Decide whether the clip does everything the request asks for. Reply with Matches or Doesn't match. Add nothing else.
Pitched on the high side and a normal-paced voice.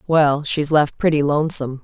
Doesn't match